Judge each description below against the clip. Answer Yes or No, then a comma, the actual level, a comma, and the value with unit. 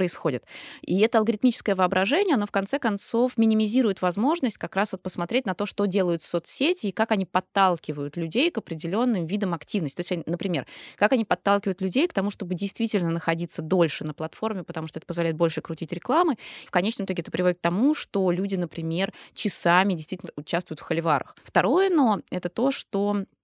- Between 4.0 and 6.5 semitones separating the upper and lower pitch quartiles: Yes, average, 4.3 semitones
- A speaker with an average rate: No, fast, 180 wpm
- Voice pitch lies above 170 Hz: Yes, high, 190 Hz